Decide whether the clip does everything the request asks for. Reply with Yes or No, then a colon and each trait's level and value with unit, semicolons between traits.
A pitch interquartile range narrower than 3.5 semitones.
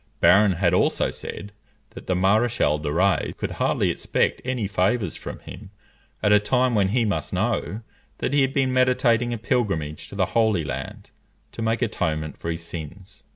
No: average, 5.0 semitones